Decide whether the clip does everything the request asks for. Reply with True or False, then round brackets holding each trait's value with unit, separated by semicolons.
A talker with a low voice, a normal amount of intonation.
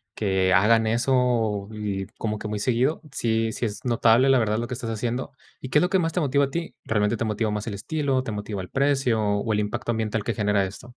True (115 Hz; 3.4 semitones)